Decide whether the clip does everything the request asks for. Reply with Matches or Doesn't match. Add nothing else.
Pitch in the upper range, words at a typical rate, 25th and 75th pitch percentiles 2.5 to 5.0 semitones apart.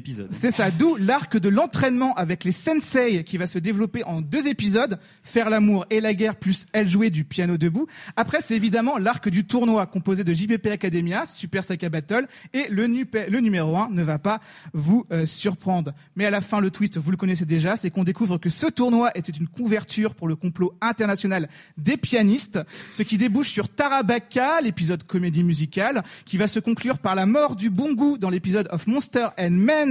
Matches